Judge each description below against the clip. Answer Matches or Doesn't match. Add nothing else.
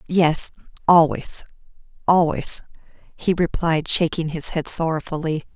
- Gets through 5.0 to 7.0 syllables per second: Doesn't match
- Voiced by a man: Doesn't match